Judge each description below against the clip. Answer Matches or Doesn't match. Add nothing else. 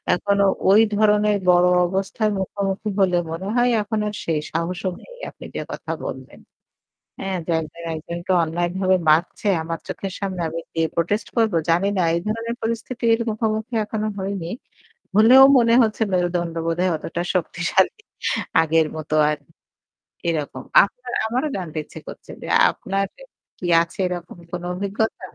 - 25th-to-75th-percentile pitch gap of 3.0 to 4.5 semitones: Matches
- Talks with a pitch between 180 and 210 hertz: Matches